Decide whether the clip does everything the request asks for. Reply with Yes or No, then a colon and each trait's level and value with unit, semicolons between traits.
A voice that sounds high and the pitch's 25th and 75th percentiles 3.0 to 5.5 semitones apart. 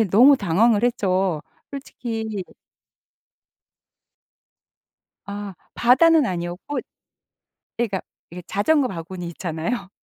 Yes: high, 205 Hz; average, 5.2 semitones